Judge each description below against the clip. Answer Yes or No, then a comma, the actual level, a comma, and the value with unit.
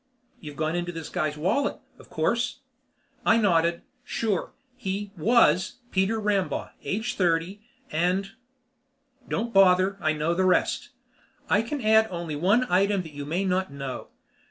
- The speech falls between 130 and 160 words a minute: Yes, average, 150 wpm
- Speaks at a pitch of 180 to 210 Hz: Yes, high, 190 Hz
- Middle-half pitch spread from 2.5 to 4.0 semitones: No, average, 4.5 semitones